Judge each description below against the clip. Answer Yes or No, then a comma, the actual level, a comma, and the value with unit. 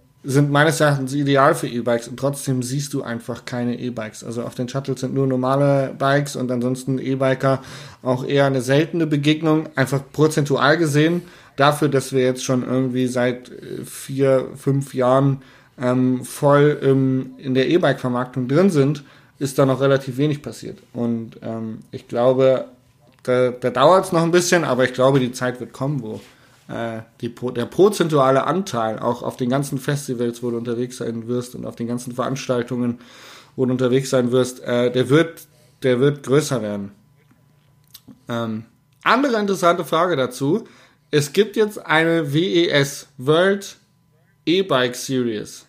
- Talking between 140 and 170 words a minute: Yes, average, 160 wpm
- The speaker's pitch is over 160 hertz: No, low, 135 Hz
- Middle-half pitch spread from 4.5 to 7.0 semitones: No, narrow, 2.5 semitones